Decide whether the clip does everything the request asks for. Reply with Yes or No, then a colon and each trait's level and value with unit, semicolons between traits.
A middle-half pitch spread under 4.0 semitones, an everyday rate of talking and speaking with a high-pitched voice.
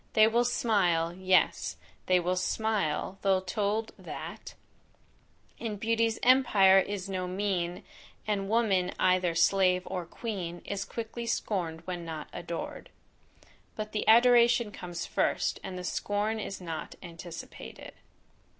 No: average, 3.5 semitones; slow, 125 wpm; high, 195 Hz